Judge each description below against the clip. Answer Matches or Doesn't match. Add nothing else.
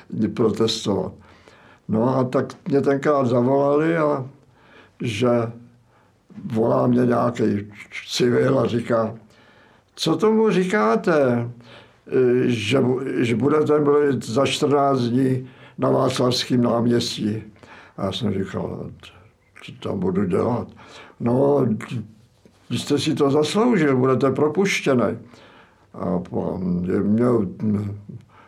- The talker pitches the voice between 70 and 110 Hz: Doesn't match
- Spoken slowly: Matches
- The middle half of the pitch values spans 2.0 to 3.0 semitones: Doesn't match